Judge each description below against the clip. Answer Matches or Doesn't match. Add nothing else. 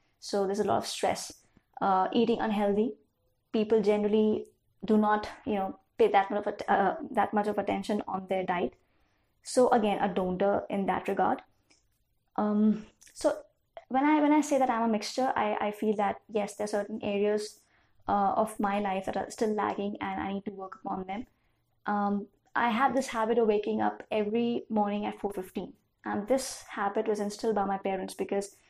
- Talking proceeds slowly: Doesn't match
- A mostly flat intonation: Matches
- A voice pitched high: Matches